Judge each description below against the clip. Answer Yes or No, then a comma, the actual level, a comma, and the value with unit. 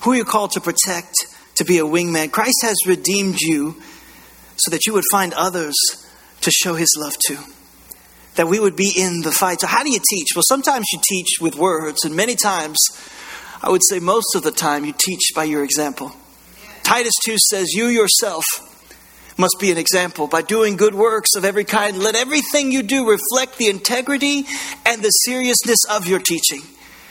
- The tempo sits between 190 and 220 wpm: Yes, average, 195 wpm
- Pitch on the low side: No, high, 190 Hz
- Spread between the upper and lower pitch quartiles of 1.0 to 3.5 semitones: No, average, 4.8 semitones